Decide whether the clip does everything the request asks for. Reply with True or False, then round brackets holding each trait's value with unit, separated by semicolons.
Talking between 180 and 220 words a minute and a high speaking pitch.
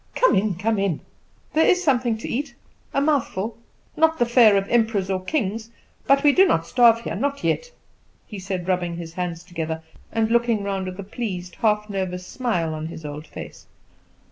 True (185 wpm; 210 Hz)